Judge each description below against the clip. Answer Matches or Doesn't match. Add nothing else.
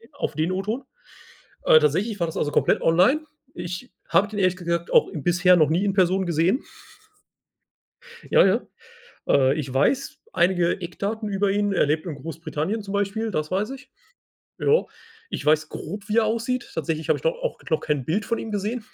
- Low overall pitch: Doesn't match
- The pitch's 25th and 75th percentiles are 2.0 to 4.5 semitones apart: Doesn't match